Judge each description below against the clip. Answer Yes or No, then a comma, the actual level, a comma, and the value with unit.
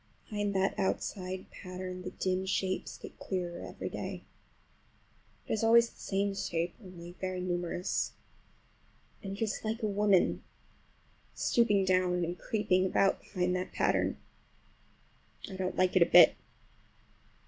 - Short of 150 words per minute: Yes, slow, 135 wpm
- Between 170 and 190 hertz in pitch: Yes, medium, 185 Hz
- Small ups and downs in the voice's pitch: Yes, narrow, 1.7 semitones